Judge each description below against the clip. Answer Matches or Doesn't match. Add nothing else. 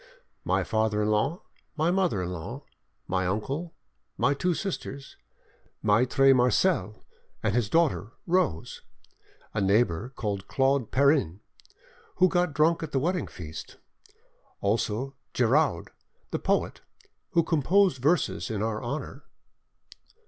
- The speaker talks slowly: Matches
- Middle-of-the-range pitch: Doesn't match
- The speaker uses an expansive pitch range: Matches